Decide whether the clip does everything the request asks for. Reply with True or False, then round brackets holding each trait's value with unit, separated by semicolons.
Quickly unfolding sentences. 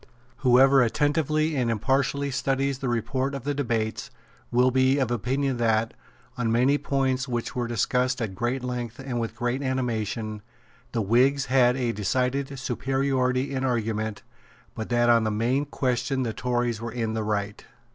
False (160 wpm)